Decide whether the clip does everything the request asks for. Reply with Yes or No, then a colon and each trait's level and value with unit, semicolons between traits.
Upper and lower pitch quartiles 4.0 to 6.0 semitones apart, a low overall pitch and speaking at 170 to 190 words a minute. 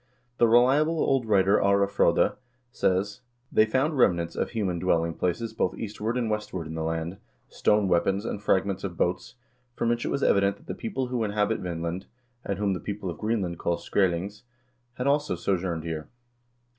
Yes: average, 4.5 semitones; low, 100 Hz; average, 180 wpm